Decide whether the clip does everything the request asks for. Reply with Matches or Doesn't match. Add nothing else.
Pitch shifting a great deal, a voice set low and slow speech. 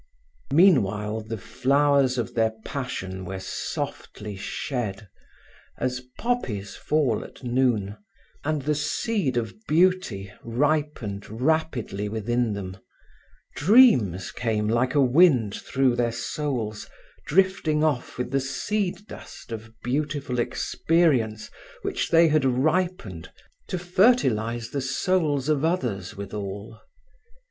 Matches